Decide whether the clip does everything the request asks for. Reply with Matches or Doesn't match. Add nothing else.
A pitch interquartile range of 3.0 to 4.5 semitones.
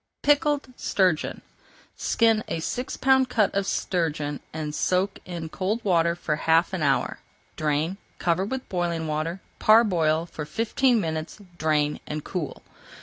Doesn't match